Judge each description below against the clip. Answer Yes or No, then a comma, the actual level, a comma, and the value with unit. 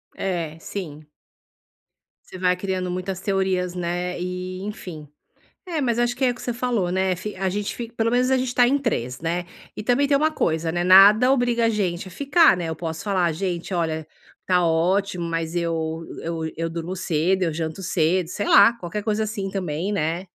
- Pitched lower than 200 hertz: Yes, medium, 185 Hz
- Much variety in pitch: No, average, 4.0 semitones